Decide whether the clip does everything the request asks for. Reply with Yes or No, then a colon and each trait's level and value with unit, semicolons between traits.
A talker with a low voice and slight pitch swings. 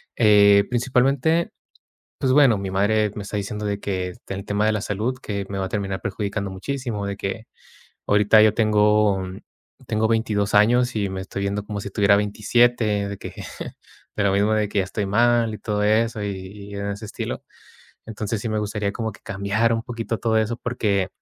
Yes: low, 105 Hz; narrow, 1.9 semitones